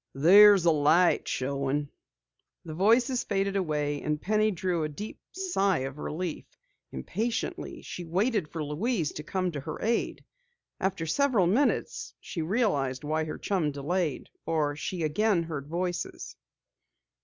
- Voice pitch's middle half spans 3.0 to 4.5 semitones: No, average, 5.1 semitones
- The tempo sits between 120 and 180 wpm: Yes, average, 140 wpm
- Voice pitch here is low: No, medium, 170 Hz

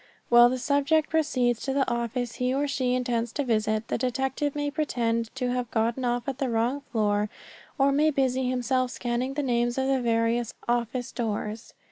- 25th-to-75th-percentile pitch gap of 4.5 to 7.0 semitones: No, narrow, 2.4 semitones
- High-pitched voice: Yes, very high, 250 Hz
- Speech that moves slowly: No, average, 185 wpm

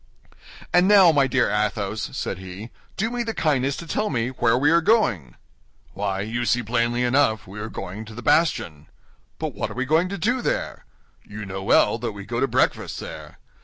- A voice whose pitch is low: Yes, low, 120 Hz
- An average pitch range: No, wide, 7.7 semitones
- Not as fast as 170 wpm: No, average, 200 wpm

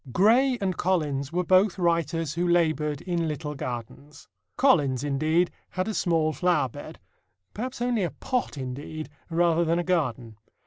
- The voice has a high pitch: No, medium, 165 Hz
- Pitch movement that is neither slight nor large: Yes, average, 3.7 semitones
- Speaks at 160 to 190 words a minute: No, average, 150 wpm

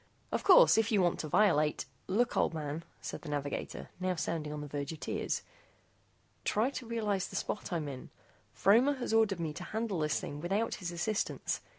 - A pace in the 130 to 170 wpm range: No, average, 200 wpm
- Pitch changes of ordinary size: No, wide, 6.3 semitones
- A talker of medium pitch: Yes, medium, 180 Hz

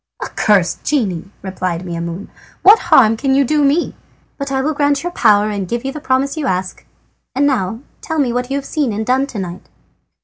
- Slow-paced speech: No, average, 200 wpm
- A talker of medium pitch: No, very high, 250 Hz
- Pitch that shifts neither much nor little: No, wide, 6.4 semitones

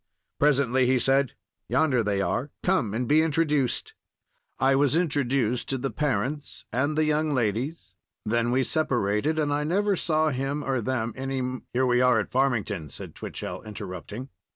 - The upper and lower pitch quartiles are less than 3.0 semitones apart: No, average, 3.6 semitones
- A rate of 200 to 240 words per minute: No, average, 165 wpm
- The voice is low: Yes, low, 130 Hz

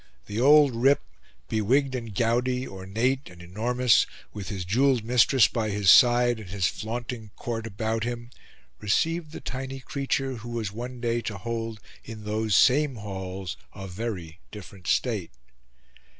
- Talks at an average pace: Yes, average, 150 wpm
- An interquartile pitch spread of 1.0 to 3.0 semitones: No, average, 3.5 semitones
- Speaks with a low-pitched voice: Yes, low, 115 Hz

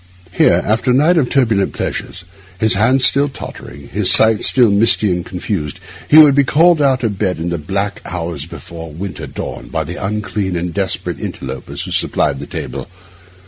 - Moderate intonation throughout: No, wide, 6.4 semitones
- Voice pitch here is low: Yes, low, 100 Hz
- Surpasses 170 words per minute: Yes, average, 185 wpm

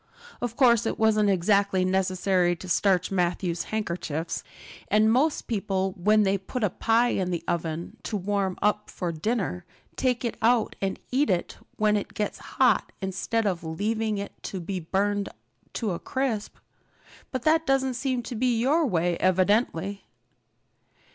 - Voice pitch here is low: No, high, 205 Hz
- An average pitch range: Yes, average, 3.8 semitones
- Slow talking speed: No, average, 155 wpm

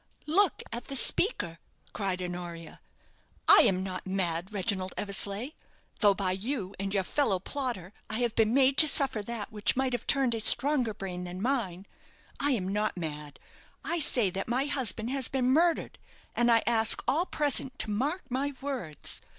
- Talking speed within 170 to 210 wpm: Yes, average, 175 wpm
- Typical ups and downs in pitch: No, wide, 6.0 semitones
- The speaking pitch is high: Yes, high, 220 Hz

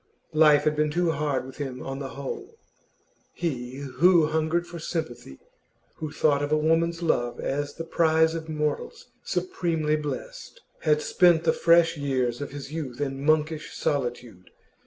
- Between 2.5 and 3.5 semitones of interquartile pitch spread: Yes, average, 2.8 semitones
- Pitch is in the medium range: Yes, medium, 150 Hz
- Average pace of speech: Yes, average, 155 wpm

